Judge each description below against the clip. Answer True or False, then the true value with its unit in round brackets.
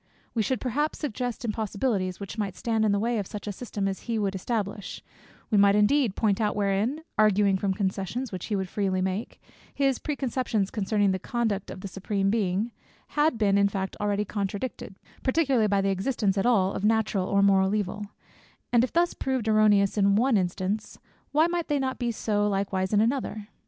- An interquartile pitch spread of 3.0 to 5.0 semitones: True (3.3 semitones)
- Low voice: False (210 Hz)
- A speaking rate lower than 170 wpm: False (195 wpm)